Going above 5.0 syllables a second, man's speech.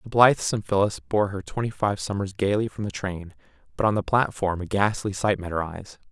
Yes: 5.7 syllables/s; male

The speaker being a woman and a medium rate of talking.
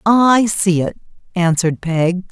No: female; slow, 130 wpm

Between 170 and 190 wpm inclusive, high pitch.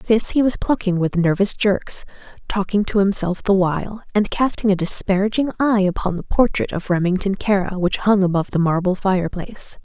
Yes: average, 175 wpm; high, 195 Hz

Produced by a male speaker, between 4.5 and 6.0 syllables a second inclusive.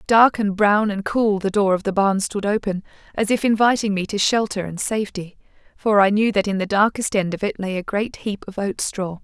No: female; 5.3 syllables/s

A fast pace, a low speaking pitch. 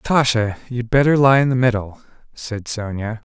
No: average, 165 wpm; low, 120 Hz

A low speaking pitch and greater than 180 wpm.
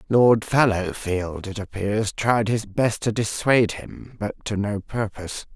No: low, 105 Hz; average, 150 wpm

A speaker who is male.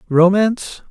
Yes: male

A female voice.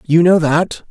No: male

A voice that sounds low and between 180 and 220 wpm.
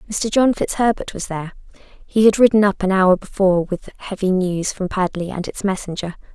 No: high, 195 Hz; average, 190 wpm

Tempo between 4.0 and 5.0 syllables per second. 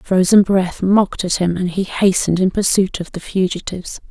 No: 5.5 syllables/s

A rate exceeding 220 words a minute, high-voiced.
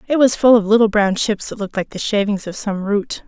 Yes: fast, 275 wpm; high, 210 Hz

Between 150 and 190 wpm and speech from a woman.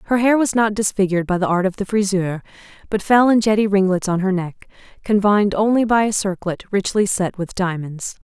No: fast, 205 wpm; female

